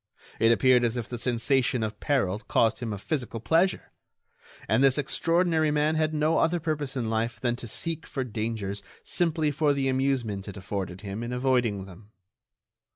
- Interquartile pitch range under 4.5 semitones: No, average, 5.1 semitones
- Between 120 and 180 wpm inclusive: Yes, average, 175 wpm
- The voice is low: Yes, low, 125 Hz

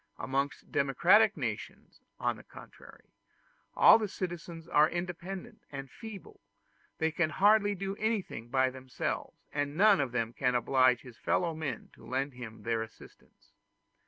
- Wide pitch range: Yes, wide, 6.7 semitones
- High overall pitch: No, medium, 150 Hz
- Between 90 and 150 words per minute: Yes, average, 145 wpm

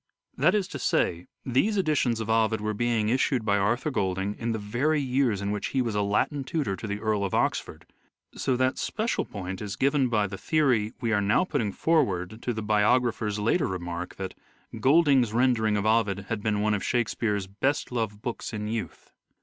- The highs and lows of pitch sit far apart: No, average, 3.9 semitones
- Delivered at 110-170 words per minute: No, average, 200 wpm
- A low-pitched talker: Yes, low, 110 Hz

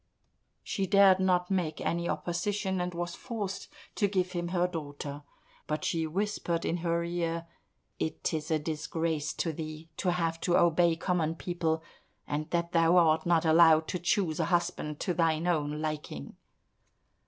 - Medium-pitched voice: Yes, medium, 170 Hz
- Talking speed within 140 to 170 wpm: Yes, average, 160 wpm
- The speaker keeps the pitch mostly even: Yes, narrow, 2.0 semitones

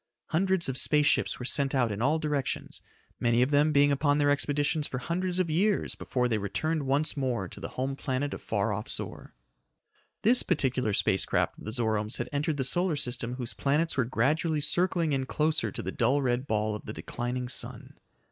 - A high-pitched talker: No, medium, 140 Hz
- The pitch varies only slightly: No, average, 3.9 semitones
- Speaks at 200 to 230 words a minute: Yes, fast, 205 wpm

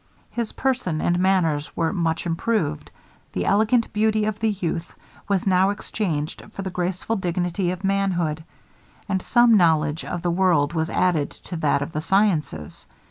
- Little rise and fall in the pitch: No, average, 3.8 semitones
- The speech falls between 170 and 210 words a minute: No, average, 160 wpm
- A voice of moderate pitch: Yes, medium, 180 Hz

